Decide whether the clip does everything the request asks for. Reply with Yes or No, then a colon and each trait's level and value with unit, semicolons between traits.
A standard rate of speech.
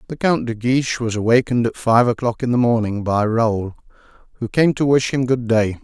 No: fast, 215 wpm